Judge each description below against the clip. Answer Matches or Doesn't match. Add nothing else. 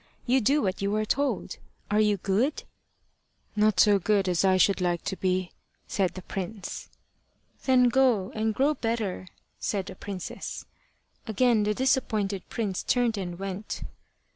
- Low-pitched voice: Doesn't match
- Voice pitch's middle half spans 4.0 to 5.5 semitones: Doesn't match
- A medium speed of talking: Matches